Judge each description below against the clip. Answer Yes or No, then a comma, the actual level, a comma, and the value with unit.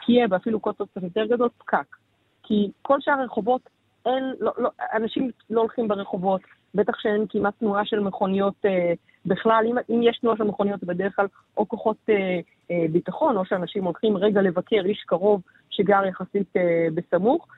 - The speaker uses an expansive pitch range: No, average, 3.0 semitones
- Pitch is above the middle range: Yes, high, 210 Hz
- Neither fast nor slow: No, fast, 165 wpm